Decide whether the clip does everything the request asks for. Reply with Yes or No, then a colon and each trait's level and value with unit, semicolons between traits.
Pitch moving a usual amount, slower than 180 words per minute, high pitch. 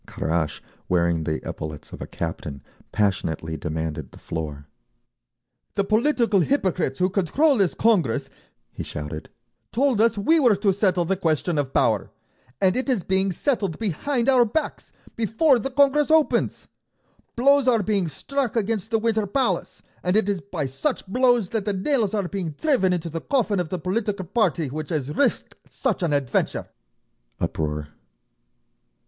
No: wide, 7.9 semitones; average, 155 wpm; high, 195 Hz